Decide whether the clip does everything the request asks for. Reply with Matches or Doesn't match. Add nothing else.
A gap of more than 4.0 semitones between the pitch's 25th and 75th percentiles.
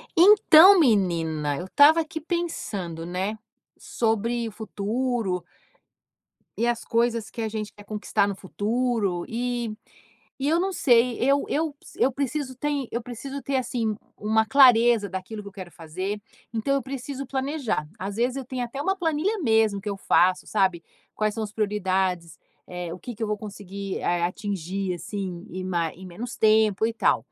Matches